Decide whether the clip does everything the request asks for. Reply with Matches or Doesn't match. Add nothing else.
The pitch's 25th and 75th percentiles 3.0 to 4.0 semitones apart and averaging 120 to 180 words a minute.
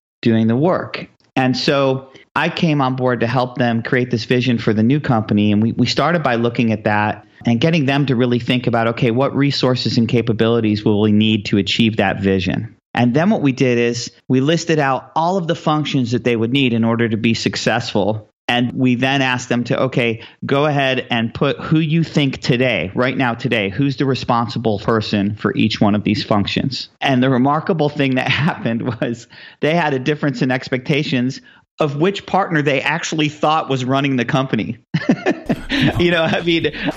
Doesn't match